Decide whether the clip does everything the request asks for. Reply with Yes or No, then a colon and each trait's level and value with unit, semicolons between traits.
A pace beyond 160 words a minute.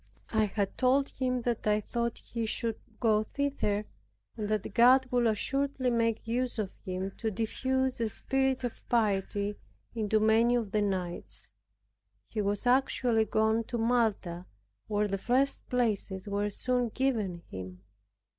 No: average, 145 wpm